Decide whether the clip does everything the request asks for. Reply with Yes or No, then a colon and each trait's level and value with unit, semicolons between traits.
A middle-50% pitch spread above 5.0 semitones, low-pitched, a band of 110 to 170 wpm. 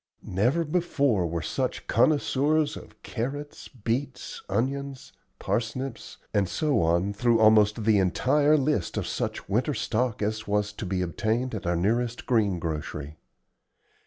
Yes: wide, 5.5 semitones; low, 115 Hz; slow, 135 wpm